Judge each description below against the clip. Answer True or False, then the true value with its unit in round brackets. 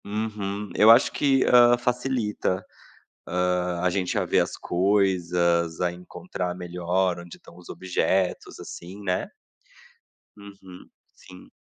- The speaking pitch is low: True (95 Hz)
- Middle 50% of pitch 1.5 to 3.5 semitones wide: True (2.9 semitones)